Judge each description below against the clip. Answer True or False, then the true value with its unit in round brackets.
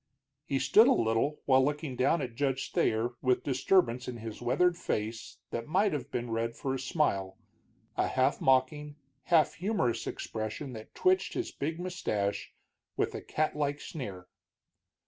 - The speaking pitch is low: True (130 Hz)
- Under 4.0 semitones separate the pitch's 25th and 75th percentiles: False (4.7 semitones)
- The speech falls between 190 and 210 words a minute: False (155 wpm)